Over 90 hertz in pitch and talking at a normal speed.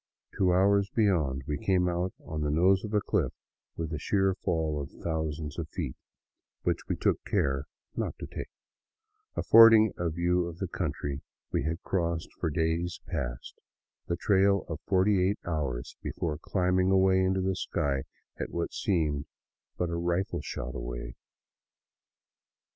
No: very low, 85 Hz; average, 160 wpm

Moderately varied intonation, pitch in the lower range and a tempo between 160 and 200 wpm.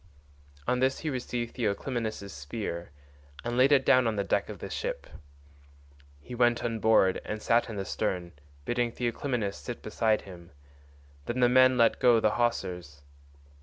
Yes: average, 3.6 semitones; low, 115 Hz; average, 165 wpm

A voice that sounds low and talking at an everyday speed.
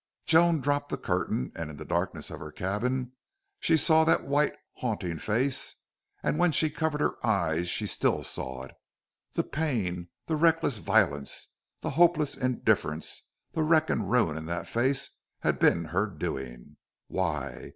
Yes: low, 120 Hz; average, 160 wpm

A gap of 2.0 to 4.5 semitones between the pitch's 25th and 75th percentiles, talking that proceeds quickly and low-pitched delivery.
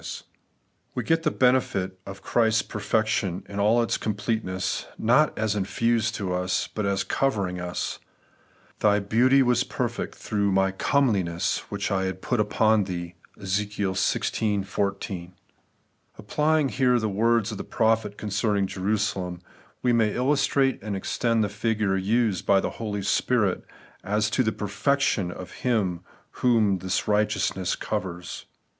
No: average, 3.2 semitones; average, 155 wpm; low, 105 Hz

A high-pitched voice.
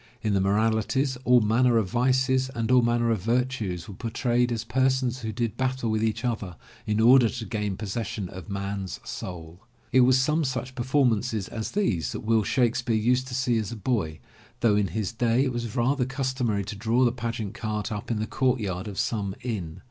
No: low, 115 Hz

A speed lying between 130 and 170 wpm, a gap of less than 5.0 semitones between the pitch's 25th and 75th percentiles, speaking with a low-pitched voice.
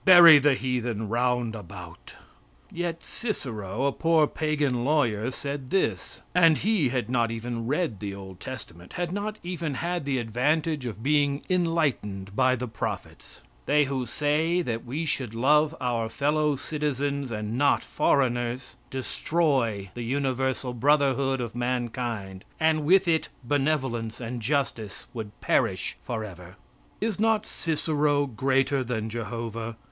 Yes: slow, 135 wpm; average, 4.6 semitones; low, 130 Hz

